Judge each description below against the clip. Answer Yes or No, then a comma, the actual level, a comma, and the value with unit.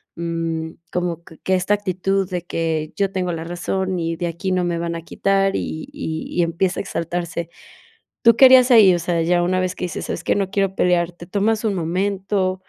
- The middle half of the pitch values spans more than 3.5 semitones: No, narrow, 2.5 semitones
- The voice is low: No, medium, 180 Hz